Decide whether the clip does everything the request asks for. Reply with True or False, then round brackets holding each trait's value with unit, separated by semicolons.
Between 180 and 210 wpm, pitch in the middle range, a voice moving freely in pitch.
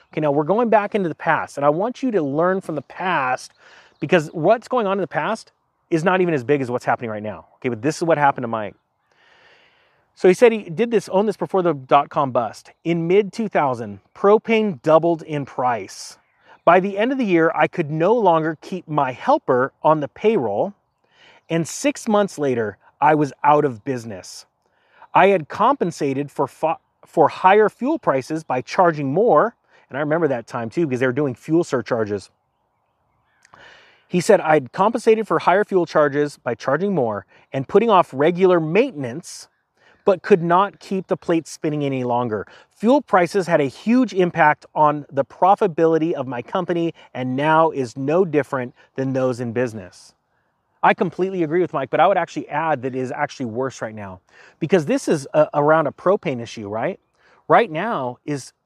True (190 wpm; 160 Hz; 5.8 semitones)